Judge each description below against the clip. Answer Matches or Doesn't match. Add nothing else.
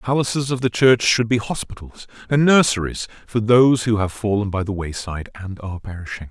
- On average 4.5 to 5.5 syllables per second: Doesn't match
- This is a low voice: Matches